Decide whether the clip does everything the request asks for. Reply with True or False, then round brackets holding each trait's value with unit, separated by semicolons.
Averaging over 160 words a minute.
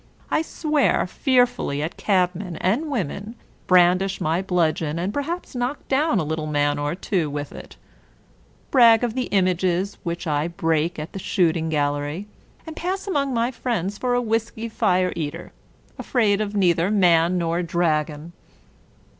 False (155 wpm)